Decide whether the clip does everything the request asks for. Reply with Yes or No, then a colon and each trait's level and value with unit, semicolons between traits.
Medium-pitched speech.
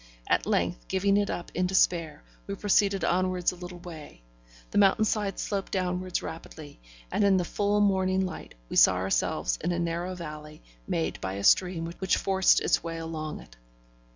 Yes: medium, 180 Hz